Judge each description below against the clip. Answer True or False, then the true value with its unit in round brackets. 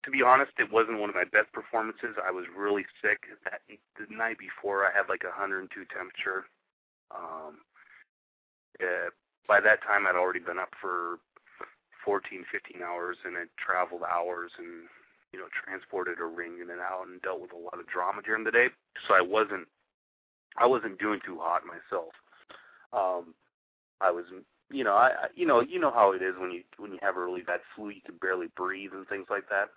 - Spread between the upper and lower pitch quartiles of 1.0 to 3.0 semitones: True (2.6 semitones)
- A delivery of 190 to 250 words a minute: True (200 wpm)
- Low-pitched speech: True (90 Hz)